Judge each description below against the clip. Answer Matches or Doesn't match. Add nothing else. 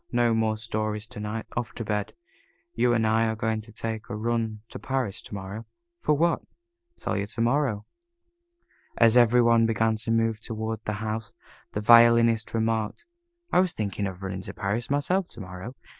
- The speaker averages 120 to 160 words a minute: Doesn't match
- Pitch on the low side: Matches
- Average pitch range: Doesn't match